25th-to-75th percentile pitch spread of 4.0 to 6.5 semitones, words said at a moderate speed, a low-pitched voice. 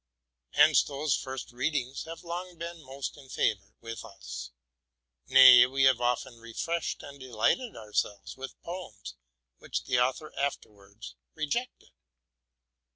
No: average, 5.0 semitones; slow, 125 wpm; low, 130 Hz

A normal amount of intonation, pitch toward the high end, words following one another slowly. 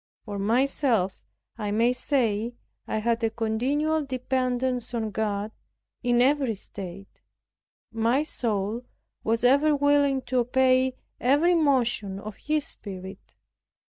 Yes: average, 3.7 semitones; high, 245 Hz; slow, 115 wpm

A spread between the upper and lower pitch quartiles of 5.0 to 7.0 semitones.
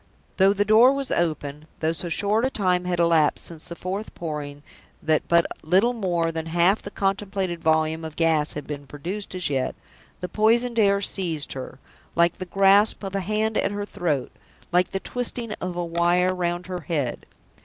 No: average, 3.8 semitones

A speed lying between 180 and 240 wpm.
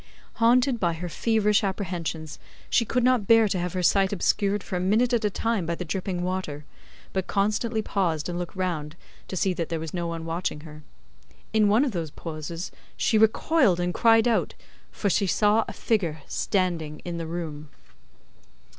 Yes: average, 185 wpm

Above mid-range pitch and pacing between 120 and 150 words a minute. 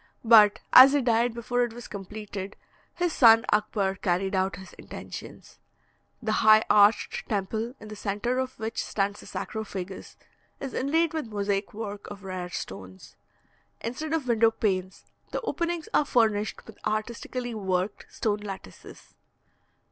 Yes: high, 215 Hz; average, 145 wpm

